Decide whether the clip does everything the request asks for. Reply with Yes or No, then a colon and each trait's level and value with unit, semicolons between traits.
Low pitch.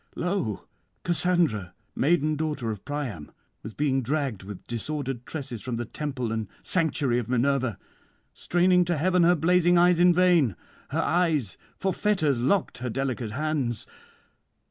No: medium, 145 Hz